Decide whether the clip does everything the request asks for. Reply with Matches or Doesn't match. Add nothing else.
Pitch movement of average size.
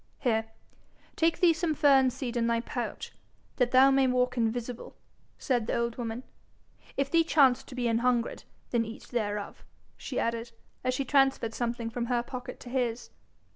Doesn't match